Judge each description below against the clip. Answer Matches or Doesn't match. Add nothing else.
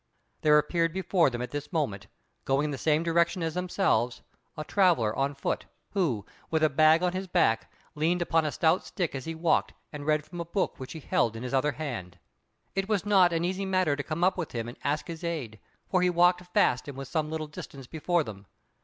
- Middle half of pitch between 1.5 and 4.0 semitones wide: Doesn't match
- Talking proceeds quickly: Matches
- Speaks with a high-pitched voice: Doesn't match